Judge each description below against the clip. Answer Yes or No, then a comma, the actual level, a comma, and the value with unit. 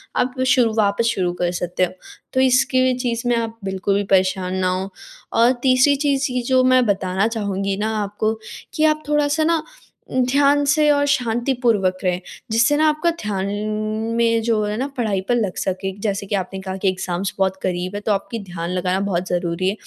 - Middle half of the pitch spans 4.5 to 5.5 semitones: Yes, average, 5.2 semitones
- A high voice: Yes, high, 215 Hz